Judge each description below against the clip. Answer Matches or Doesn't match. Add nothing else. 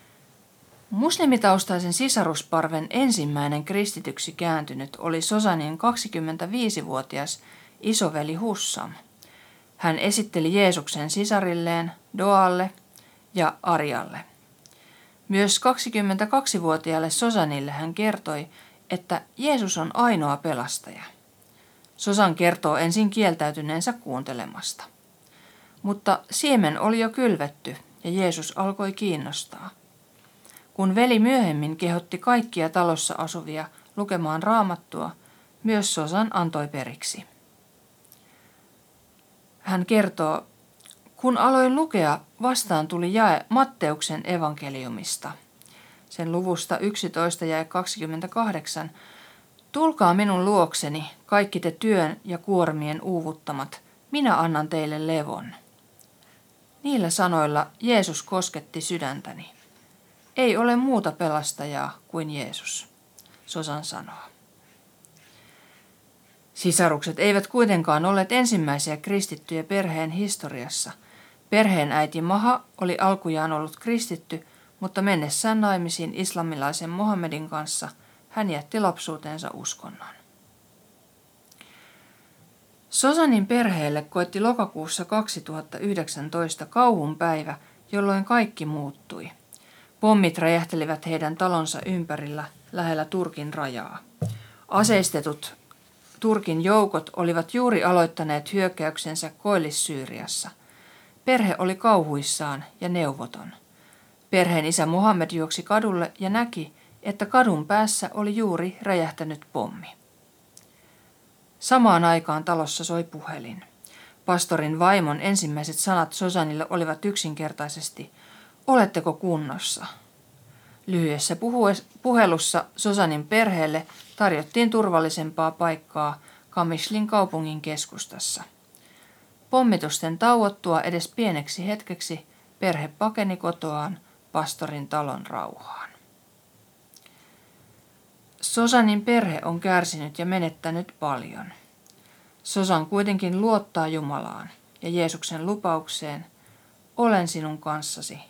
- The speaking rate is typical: Doesn't match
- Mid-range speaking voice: Matches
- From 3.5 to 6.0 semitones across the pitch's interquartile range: Matches